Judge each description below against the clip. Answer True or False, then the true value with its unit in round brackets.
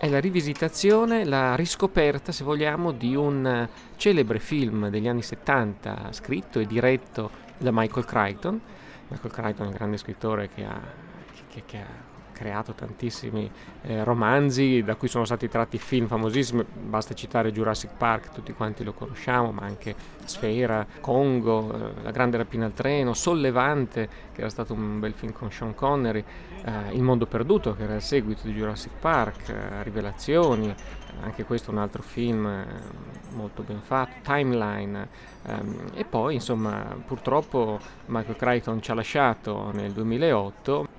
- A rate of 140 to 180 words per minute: True (160 wpm)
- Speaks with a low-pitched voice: True (115 Hz)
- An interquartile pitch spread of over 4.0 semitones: False (3.5 semitones)